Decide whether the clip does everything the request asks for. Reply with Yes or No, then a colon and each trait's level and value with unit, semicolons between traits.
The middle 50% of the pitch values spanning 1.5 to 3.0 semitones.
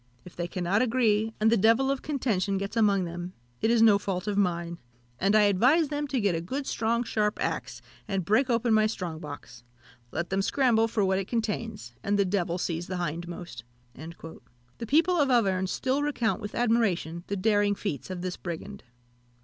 No: average, 4.5 semitones